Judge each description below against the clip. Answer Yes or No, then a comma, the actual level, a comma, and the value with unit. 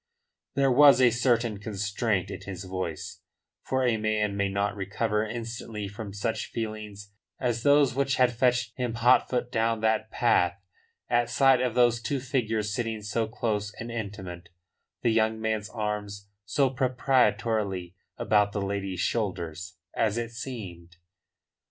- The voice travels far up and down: No, average, 2.9 semitones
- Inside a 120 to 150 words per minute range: Yes, average, 145 wpm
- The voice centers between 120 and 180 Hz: No, low, 110 Hz